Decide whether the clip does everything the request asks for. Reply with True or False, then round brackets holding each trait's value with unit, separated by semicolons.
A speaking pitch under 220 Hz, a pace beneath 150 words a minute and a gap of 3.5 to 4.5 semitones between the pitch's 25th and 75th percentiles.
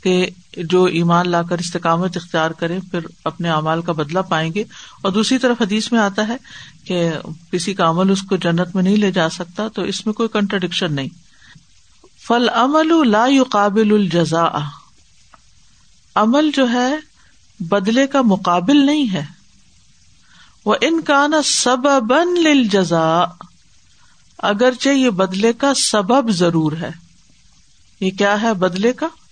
False (195 Hz; 140 wpm; 5.6 semitones)